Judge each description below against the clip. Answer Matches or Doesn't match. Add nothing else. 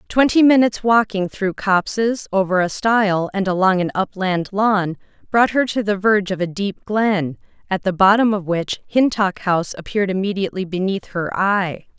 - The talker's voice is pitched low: Doesn't match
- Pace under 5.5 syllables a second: Matches